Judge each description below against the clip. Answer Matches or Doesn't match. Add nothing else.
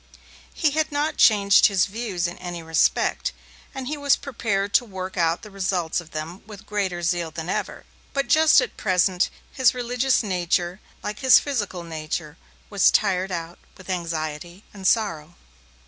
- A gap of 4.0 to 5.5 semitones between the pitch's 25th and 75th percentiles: Matches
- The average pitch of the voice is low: Doesn't match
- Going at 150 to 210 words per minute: Matches